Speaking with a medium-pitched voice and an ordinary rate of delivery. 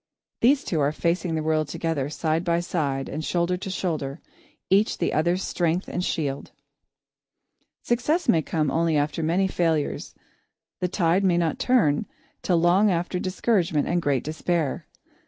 Yes: medium, 170 Hz; average, 155 wpm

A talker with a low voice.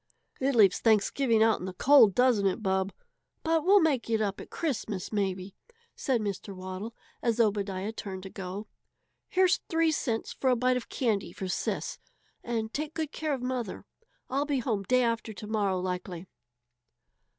No: high, 225 Hz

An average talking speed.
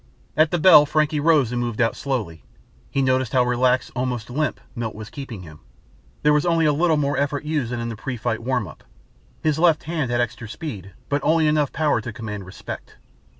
No: fast, 210 wpm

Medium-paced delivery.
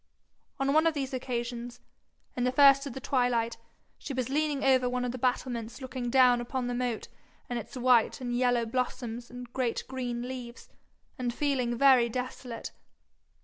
Yes: average, 170 wpm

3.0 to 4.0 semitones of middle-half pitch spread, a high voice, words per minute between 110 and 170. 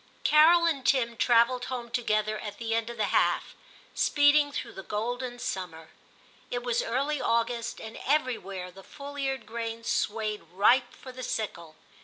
Yes: average, 3.3 semitones; high, 235 Hz; average, 160 wpm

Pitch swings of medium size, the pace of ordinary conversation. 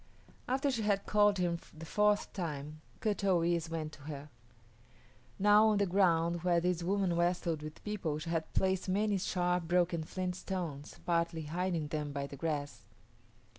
Yes: average, 3.4 semitones; average, 170 wpm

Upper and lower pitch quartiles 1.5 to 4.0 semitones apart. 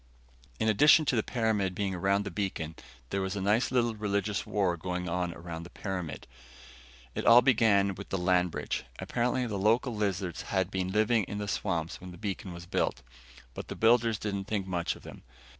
Yes: average, 3.2 semitones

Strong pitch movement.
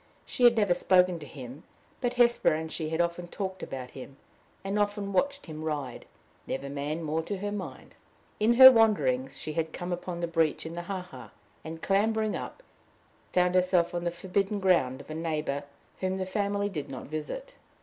No: average, 4.6 semitones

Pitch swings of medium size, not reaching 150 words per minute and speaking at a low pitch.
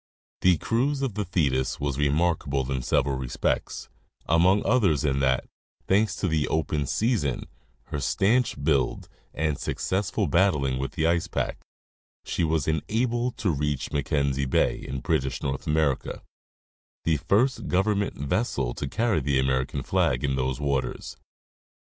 No: wide, 6.0 semitones; average, 140 wpm; very low, 75 Hz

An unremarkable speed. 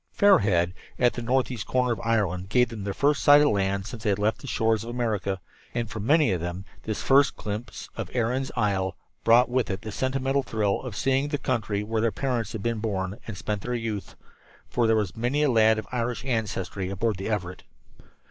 No: fast, 215 wpm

